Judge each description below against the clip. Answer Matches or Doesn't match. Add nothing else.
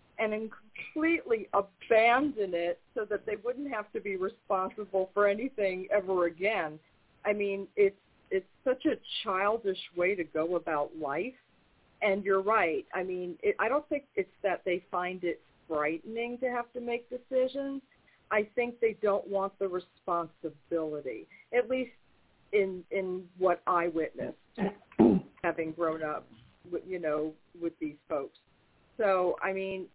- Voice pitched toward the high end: Matches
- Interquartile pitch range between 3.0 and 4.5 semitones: Doesn't match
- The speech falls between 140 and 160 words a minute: Matches